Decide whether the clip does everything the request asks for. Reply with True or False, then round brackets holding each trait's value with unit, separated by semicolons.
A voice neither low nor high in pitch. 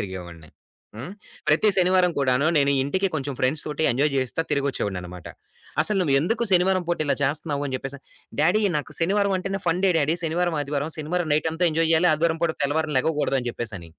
True (155 Hz)